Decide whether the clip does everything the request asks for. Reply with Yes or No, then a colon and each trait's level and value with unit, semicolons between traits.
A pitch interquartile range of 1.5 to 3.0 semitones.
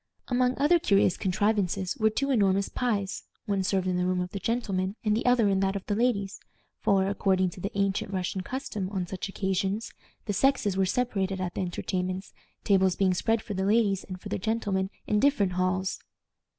Yes: narrow, 2.5 semitones